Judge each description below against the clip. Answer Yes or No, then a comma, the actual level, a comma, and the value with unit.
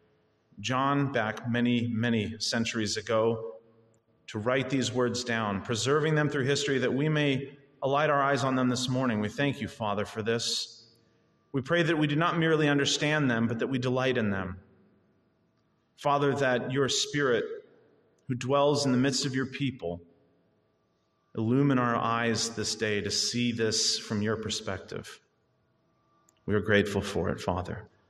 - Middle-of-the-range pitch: No, low, 120 Hz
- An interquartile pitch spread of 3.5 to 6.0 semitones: Yes, average, 4.1 semitones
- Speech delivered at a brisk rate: No, average, 160 wpm